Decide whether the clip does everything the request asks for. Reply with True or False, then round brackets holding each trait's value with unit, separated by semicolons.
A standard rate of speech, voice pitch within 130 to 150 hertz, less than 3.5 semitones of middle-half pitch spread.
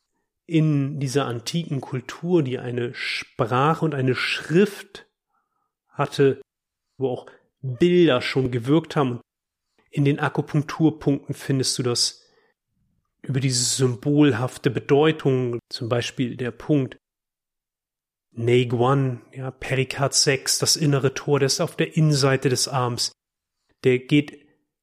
False (115 wpm; 135 Hz; 3.0 semitones)